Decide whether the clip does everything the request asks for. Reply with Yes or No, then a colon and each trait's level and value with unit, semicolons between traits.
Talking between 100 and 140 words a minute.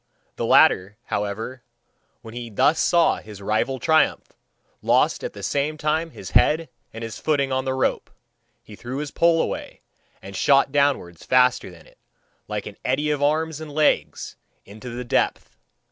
No: average, 165 wpm